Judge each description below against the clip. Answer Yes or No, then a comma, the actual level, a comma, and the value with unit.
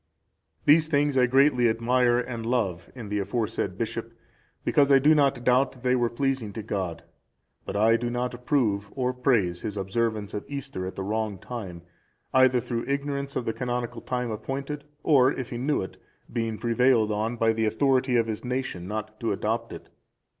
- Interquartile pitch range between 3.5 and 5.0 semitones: No, average, 3.1 semitones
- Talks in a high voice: No, low, 120 Hz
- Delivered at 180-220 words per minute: Yes, average, 185 wpm